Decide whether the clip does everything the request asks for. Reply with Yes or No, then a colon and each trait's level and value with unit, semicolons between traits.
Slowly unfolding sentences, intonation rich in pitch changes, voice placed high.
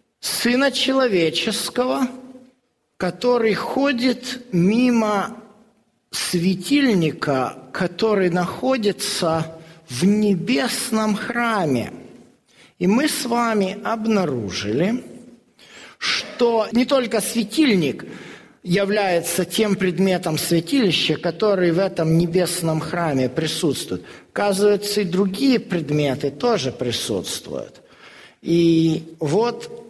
Yes: slow, 75 wpm; wide, 5.7 semitones; high, 205 Hz